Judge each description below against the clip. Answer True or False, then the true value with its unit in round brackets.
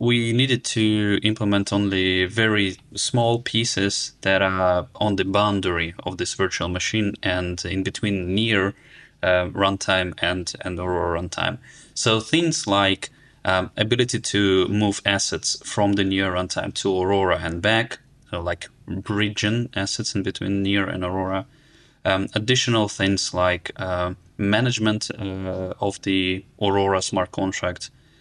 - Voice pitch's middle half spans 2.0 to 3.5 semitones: True (2.7 semitones)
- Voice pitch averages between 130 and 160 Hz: False (100 Hz)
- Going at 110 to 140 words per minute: True (135 wpm)